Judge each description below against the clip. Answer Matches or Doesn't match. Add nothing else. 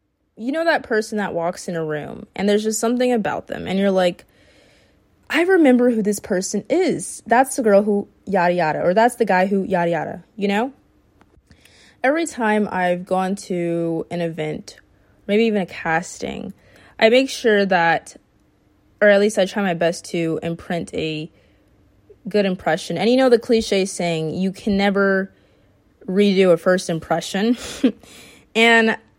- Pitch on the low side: Doesn't match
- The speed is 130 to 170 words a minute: Matches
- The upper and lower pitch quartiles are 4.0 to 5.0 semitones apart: Matches